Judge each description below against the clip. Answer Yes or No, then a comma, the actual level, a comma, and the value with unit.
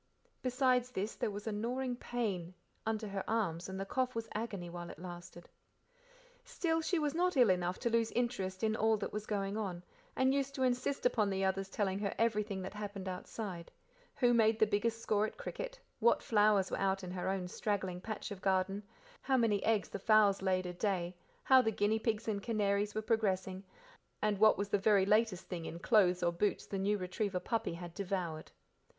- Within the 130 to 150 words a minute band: No, average, 200 wpm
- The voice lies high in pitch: Yes, high, 205 Hz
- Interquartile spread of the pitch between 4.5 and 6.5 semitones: No, average, 3.1 semitones